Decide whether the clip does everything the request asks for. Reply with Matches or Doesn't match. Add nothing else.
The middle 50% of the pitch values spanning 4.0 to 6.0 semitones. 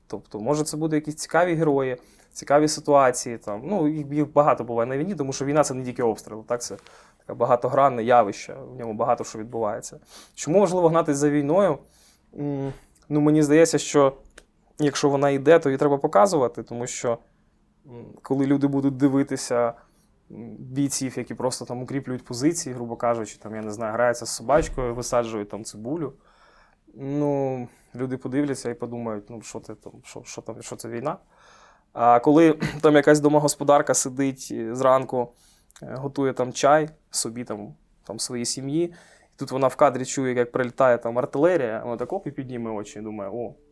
Doesn't match